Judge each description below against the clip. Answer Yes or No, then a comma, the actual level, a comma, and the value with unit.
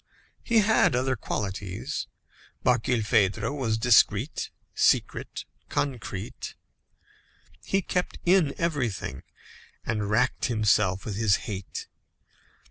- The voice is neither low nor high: No, low, 115 Hz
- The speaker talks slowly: Yes, slow, 90 wpm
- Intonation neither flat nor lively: Yes, average, 4.6 semitones